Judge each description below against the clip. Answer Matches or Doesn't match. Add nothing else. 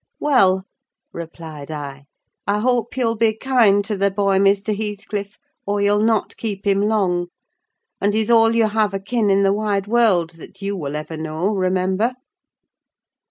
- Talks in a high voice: Matches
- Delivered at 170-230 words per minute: Doesn't match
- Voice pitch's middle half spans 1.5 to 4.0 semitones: Matches